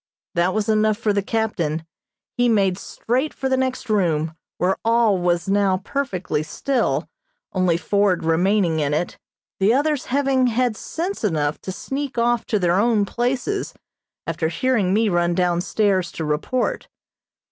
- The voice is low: No, high, 205 Hz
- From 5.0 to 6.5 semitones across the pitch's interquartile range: Yes, wide, 5.6 semitones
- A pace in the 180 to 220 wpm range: No, average, 155 wpm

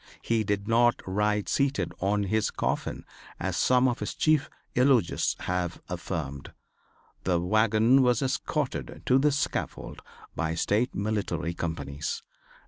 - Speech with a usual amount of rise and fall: No, wide, 5.9 semitones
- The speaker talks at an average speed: No, slow, 130 wpm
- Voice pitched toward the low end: Yes, low, 110 Hz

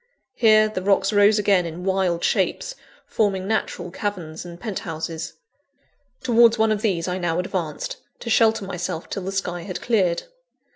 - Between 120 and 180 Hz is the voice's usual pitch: No, high, 190 Hz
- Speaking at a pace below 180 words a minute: Yes, average, 155 wpm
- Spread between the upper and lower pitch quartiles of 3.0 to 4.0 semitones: Yes, average, 3.6 semitones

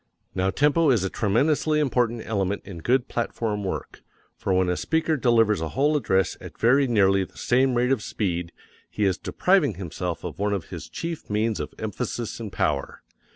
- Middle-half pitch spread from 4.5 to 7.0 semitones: Yes, wide, 5.4 semitones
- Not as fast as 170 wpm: No, average, 185 wpm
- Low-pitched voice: Yes, low, 110 Hz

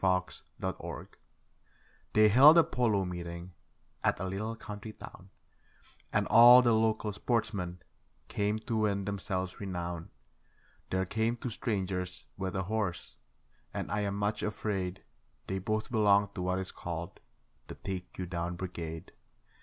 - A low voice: Yes, low, 100 Hz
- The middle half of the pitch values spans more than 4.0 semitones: No, average, 2.9 semitones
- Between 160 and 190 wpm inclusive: No, average, 145 wpm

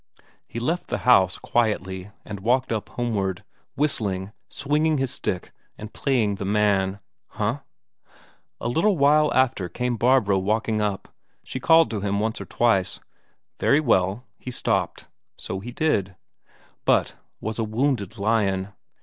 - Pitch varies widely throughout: No, average, 4.7 semitones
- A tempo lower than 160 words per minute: Yes, average, 140 wpm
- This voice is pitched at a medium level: No, low, 110 Hz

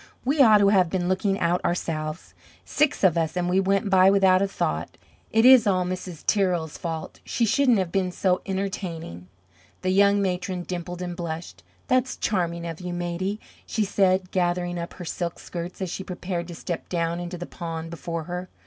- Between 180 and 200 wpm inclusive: Yes, average, 190 wpm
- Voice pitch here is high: No, medium, 180 Hz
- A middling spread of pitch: No, narrow, 2.3 semitones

